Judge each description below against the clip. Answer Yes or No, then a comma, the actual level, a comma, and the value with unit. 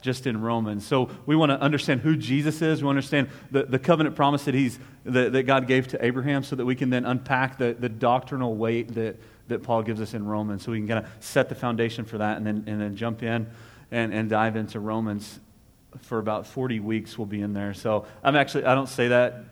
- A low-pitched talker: Yes, low, 120 Hz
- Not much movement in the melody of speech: No, average, 3.4 semitones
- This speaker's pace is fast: Yes, fast, 245 wpm